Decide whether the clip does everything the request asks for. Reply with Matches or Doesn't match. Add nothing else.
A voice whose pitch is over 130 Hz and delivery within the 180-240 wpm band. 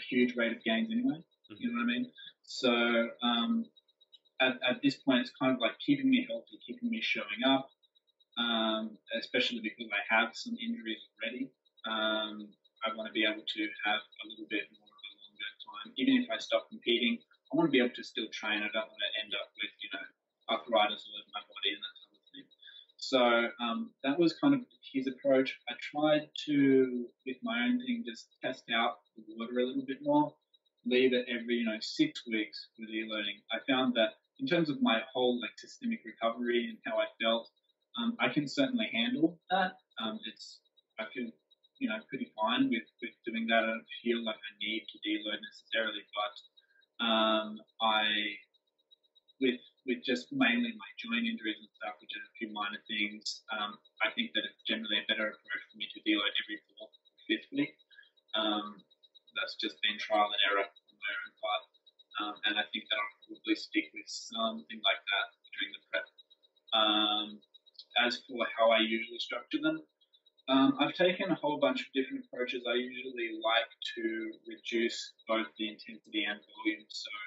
Doesn't match